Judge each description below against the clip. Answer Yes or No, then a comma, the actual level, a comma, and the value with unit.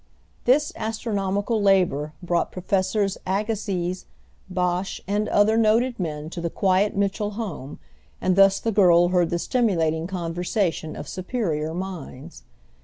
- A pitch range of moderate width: Yes, average, 3.3 semitones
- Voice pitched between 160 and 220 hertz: Yes, high, 190 Hz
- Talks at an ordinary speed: No, slow, 125 wpm